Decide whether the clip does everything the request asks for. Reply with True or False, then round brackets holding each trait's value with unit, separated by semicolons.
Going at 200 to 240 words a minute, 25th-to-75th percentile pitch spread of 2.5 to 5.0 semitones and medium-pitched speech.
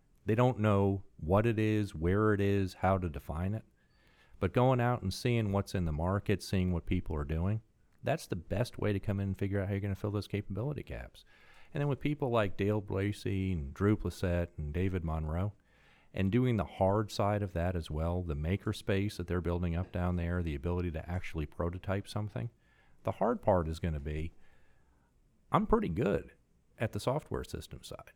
False (205 wpm; 3.2 semitones; 95 Hz)